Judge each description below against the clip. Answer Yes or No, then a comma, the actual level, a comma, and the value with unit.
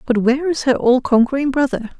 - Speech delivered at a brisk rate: Yes, fast, 210 wpm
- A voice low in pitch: No, very high, 260 Hz